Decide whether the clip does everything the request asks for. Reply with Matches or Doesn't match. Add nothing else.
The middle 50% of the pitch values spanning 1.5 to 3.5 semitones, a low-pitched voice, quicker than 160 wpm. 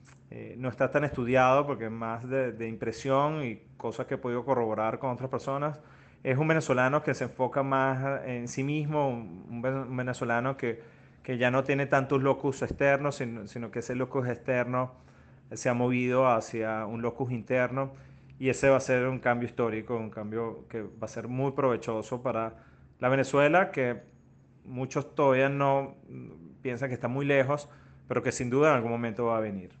Matches